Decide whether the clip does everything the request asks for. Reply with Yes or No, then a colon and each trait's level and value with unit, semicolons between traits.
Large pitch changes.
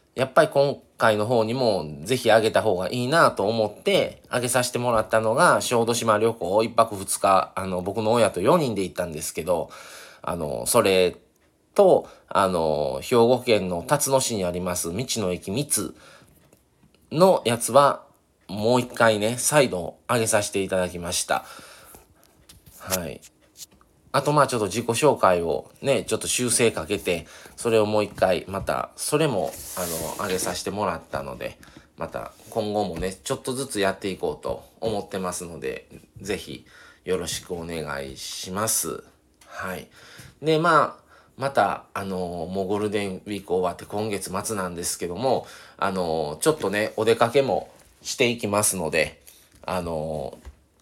No: average, 4.4 semitones